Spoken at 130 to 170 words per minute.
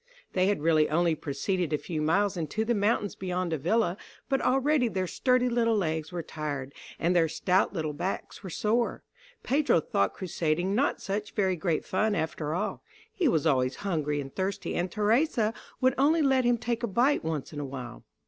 No: average, 185 wpm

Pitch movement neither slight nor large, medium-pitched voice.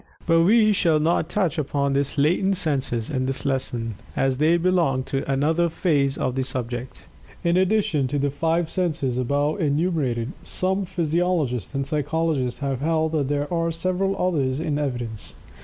Yes: average, 4.1 semitones; medium, 150 Hz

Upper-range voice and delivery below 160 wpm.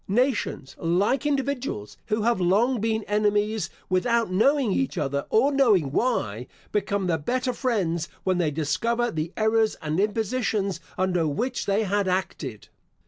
Yes: high, 205 Hz; average, 140 wpm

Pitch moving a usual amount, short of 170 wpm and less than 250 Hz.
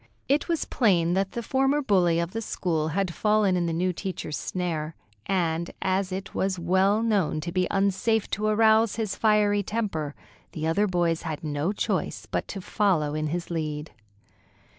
No: average, 4.1 semitones; average, 175 wpm; medium, 185 Hz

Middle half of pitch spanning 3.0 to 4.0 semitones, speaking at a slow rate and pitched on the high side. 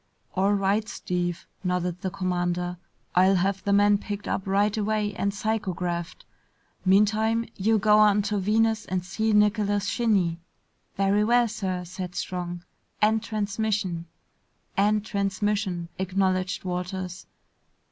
No: narrow, 2.6 semitones; slow, 125 wpm; high, 200 Hz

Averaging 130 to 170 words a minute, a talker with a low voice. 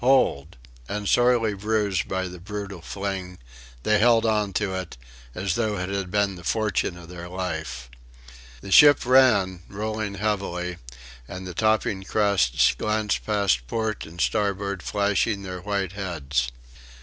Yes: average, 145 wpm; low, 100 Hz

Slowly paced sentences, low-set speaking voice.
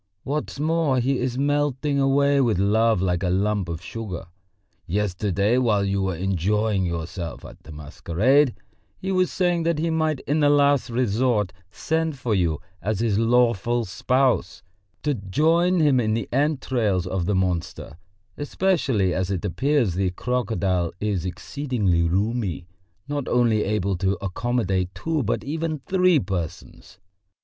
No: average, 145 wpm; low, 115 Hz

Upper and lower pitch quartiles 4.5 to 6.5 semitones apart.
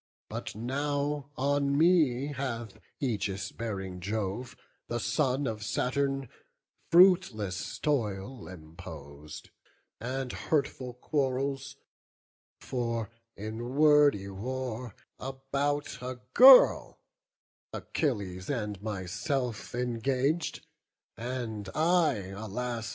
Yes: average, 4.9 semitones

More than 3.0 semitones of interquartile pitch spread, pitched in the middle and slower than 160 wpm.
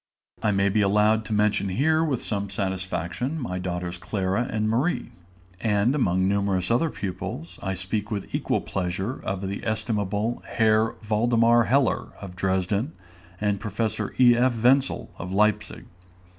No: average, 3.5 semitones; low, 105 Hz; average, 145 wpm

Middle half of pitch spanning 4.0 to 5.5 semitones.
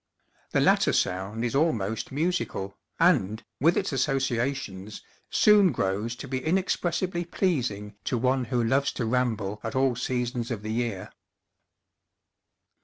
Yes: average, 4.3 semitones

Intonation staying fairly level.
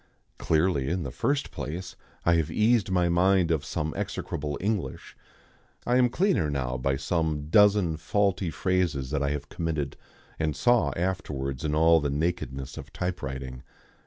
No: average, 4.6 semitones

